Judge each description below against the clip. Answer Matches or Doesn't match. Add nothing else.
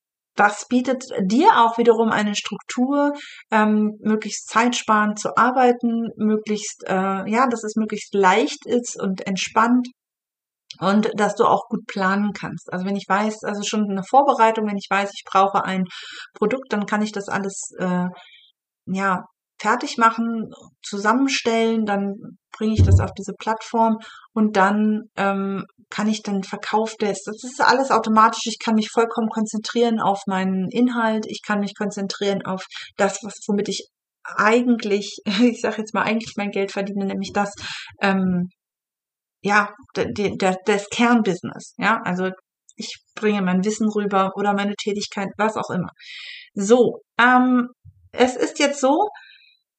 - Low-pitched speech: Doesn't match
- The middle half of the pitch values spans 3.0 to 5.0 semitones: Doesn't match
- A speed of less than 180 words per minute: Matches